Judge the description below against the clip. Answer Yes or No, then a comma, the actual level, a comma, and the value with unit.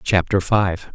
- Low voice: Yes, very low, 90 Hz